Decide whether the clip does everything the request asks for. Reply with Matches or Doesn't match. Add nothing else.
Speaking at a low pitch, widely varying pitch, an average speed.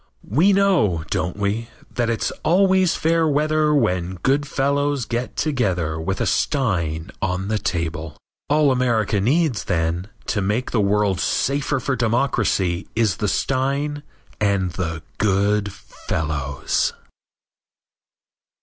Doesn't match